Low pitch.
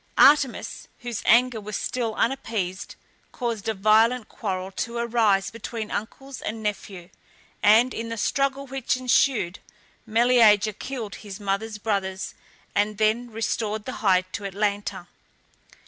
No: high, 220 Hz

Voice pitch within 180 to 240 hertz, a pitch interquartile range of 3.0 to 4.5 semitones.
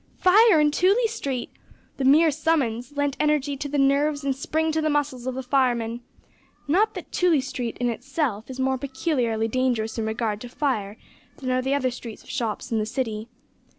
No: very high, 265 Hz; average, 3.8 semitones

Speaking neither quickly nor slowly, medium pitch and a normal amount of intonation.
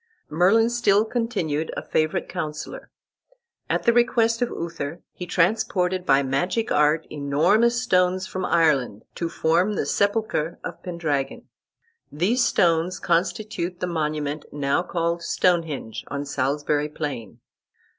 No: slow, 125 wpm; medium, 170 Hz; average, 4.8 semitones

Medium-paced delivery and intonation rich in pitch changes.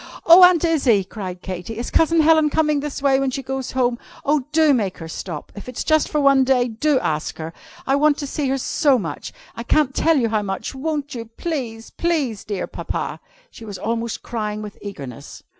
No: fast, 210 wpm; wide, 5.8 semitones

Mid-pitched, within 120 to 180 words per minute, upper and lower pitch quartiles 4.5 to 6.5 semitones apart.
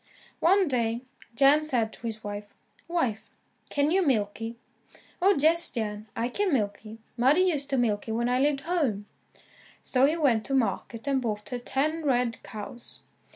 No: very high, 250 Hz; average, 175 wpm; average, 5.0 semitones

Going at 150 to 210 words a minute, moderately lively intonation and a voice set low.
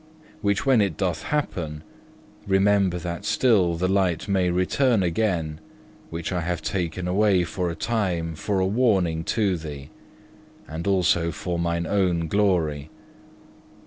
No: average, 140 wpm; average, 3.1 semitones; very low, 90 Hz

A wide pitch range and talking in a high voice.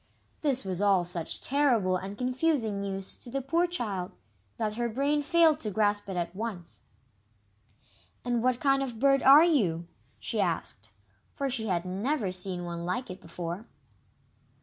Yes: wide, 6.7 semitones; high, 220 Hz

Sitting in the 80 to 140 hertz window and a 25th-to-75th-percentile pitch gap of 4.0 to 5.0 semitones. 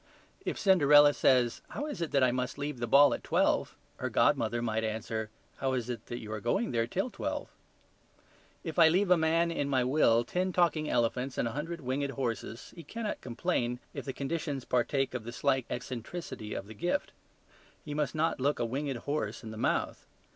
Yes: low, 135 Hz; average, 4.7 semitones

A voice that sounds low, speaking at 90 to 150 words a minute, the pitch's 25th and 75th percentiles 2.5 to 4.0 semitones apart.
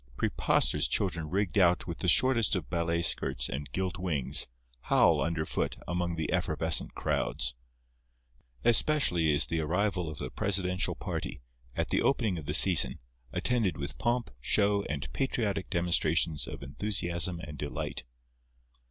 No: very low, 85 Hz; average, 140 wpm; average, 4.4 semitones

